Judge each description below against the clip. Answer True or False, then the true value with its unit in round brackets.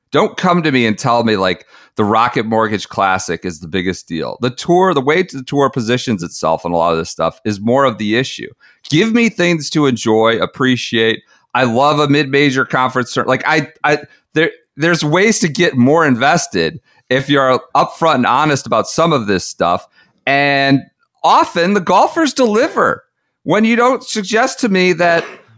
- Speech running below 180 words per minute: False (185 wpm)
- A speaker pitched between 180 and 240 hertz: False (140 Hz)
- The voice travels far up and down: True (7.6 semitones)